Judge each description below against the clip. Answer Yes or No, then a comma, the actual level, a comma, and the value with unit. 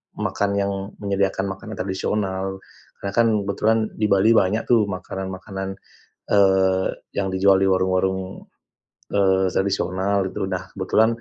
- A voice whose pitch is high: No, very low, 95 Hz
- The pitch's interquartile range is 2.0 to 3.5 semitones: No, narrow, 1.0 semitones